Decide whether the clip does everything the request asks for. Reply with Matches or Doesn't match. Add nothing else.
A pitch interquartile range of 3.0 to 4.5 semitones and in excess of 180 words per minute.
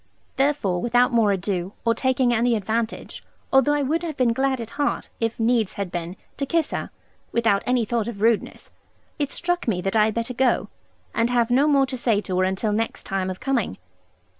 Matches